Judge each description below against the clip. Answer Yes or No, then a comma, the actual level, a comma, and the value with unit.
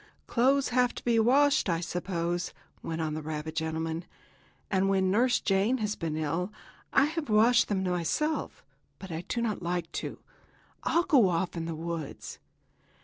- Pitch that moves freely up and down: Yes, wide, 6.4 semitones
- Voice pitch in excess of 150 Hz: Yes, high, 190 Hz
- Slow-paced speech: No, average, 165 wpm